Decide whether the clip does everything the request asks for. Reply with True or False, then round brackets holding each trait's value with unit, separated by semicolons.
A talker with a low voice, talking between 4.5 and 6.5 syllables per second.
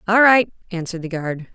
False (190 Hz; 5.8 syllables/s)